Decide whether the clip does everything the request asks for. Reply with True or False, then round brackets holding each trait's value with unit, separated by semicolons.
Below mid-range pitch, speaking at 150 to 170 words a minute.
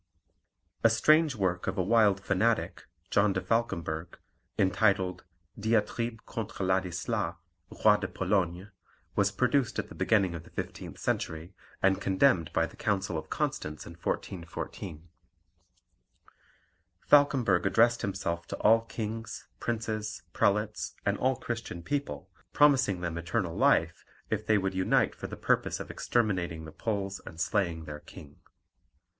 False (100 Hz; 135 wpm)